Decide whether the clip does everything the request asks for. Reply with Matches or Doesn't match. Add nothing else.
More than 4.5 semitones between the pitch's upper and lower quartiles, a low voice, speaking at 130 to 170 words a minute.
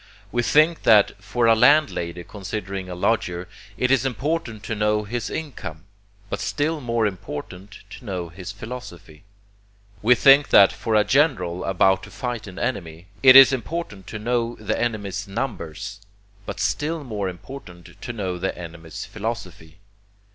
Matches